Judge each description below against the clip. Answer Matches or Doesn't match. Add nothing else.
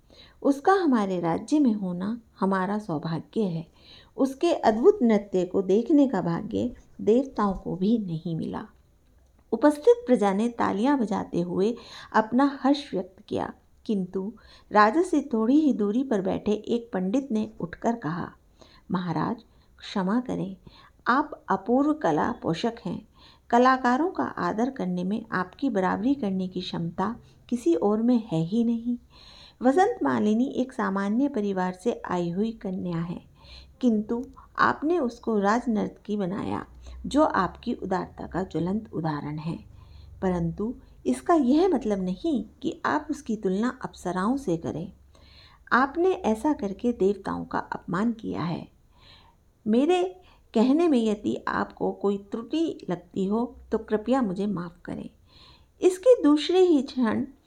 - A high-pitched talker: Matches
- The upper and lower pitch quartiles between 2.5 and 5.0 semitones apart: Doesn't match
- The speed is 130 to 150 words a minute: Matches